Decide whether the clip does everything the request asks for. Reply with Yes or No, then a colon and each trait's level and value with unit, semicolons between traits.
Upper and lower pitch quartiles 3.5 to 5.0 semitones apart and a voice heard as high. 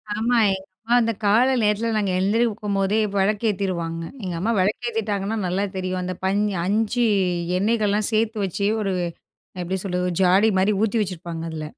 No: average, 2.9 semitones; high, 200 Hz